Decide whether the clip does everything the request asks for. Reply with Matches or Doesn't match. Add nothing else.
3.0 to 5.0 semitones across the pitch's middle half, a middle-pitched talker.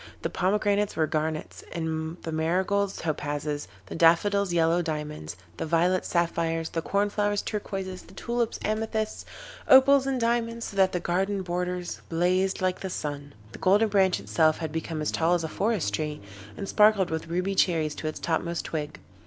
Matches